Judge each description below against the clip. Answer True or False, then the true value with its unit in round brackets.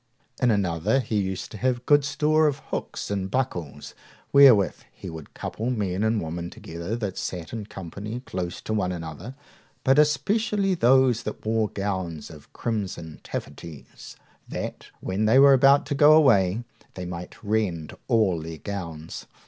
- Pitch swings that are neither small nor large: False (6.6 semitones)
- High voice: False (105 Hz)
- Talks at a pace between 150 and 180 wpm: True (155 wpm)